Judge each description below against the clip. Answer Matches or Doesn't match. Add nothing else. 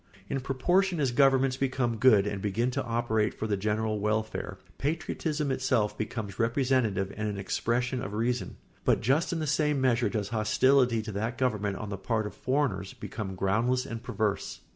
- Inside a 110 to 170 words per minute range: Doesn't match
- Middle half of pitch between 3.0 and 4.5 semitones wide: Matches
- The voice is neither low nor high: Doesn't match